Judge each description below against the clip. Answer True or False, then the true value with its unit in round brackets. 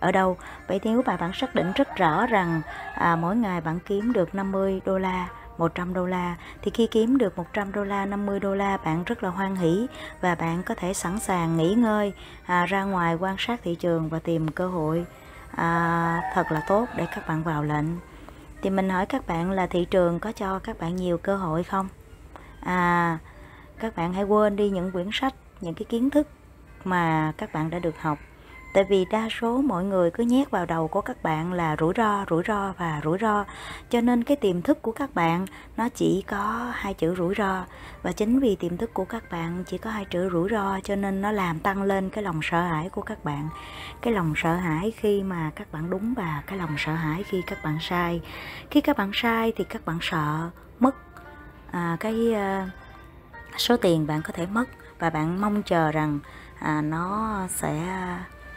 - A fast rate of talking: False (215 wpm)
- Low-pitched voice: False (185 Hz)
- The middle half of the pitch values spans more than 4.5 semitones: False (3.8 semitones)